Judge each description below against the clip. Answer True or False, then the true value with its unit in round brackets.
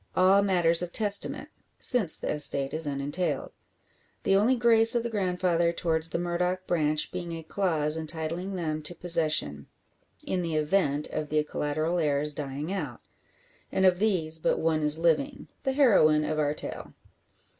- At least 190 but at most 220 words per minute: False (160 wpm)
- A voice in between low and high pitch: True (165 Hz)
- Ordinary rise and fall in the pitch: True (3.4 semitones)